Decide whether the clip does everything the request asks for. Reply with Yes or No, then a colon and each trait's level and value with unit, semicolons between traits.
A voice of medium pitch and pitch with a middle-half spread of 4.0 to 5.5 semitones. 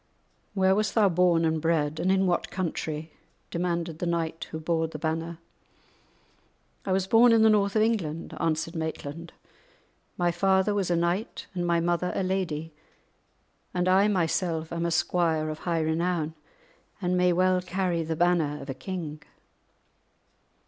No: medium, 170 Hz; narrow, 2.5 semitones